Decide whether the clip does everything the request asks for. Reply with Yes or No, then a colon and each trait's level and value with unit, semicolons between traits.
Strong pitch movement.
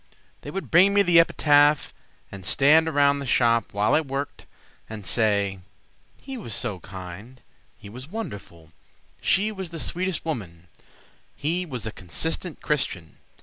Yes: wide, 8.4 semitones